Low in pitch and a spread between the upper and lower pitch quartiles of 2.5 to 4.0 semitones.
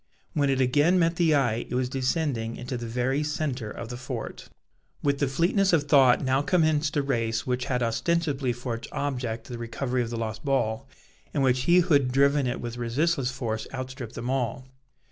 Yes: low, 130 Hz; average, 3.3 semitones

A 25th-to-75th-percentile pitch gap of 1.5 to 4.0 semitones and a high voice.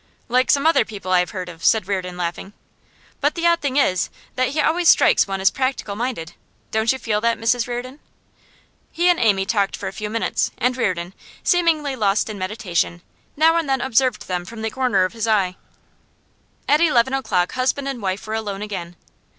No: wide, 5.5 semitones; high, 225 Hz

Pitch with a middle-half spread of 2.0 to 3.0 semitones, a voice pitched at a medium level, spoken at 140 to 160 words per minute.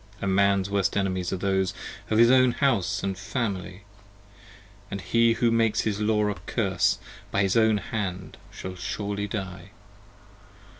No: narrow, 2.4 semitones; low, 100 Hz; average, 155 wpm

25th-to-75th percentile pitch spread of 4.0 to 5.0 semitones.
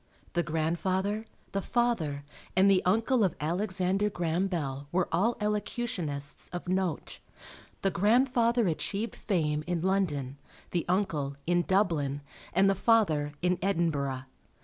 Yes: average, 4.4 semitones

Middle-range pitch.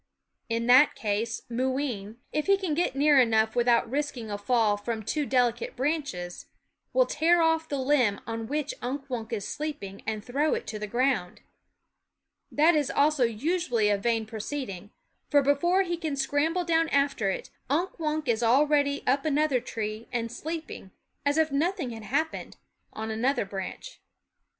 No: very high, 260 Hz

